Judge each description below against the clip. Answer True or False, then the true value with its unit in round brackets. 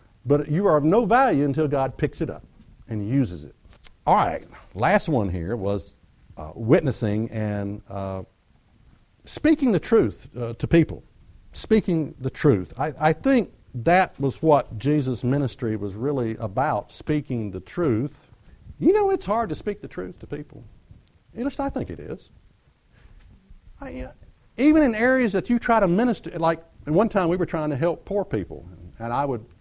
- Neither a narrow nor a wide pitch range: False (8.2 semitones)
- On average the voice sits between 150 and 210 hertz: False (140 Hz)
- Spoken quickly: False (175 wpm)